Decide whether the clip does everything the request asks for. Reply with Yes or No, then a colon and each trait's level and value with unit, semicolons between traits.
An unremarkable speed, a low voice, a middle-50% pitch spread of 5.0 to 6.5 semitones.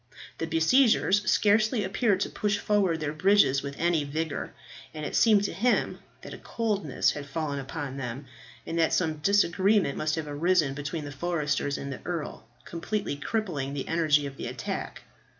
No: average, 170 wpm; medium, 160 Hz; wide, 5.6 semitones